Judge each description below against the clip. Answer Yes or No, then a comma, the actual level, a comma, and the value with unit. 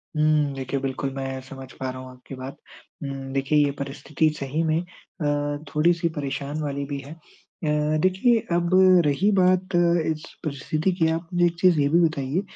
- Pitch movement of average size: Yes, average, 3.1 semitones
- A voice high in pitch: No, medium, 150 Hz